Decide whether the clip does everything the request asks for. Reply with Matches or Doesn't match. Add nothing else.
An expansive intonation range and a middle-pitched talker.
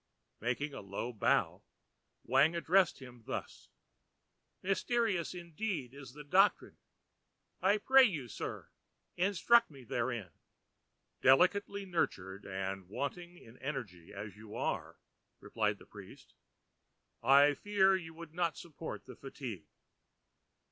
Matches